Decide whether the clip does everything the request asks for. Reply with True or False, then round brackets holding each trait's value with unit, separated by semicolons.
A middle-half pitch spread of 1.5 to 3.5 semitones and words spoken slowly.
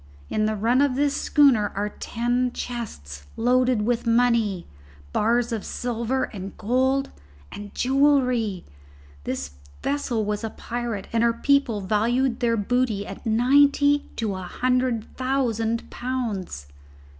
True (3.2 semitones; 130 wpm)